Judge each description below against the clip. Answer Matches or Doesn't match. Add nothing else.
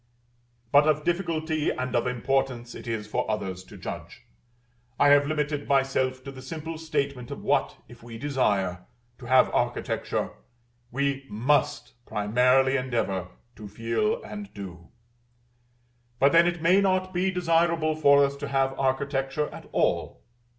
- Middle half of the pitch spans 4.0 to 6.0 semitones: Matches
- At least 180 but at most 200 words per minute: Doesn't match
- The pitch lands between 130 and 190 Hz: Matches